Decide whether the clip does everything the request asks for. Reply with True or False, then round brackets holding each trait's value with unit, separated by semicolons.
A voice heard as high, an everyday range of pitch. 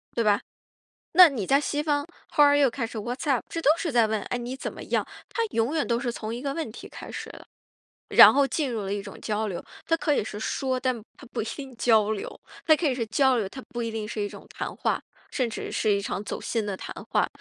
True (240 Hz; 4.4 semitones)